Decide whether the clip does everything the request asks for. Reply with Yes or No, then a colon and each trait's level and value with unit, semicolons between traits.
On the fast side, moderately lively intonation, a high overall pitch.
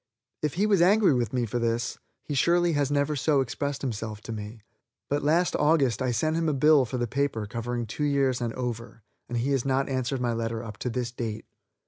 No: fast, 220 wpm; average, 3.8 semitones; low, 130 Hz